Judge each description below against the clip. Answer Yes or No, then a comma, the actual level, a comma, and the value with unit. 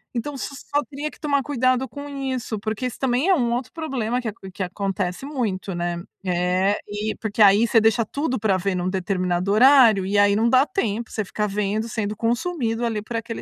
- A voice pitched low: No, high, 225 Hz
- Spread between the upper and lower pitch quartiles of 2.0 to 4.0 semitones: No, average, 4.4 semitones